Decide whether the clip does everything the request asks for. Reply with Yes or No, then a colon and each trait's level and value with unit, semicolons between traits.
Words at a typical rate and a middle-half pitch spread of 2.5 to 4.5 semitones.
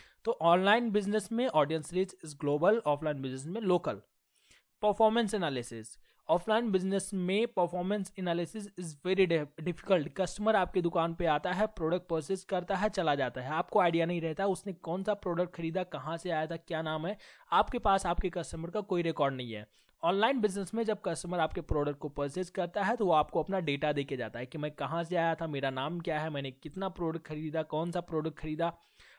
No: fast, 200 wpm; average, 3.8 semitones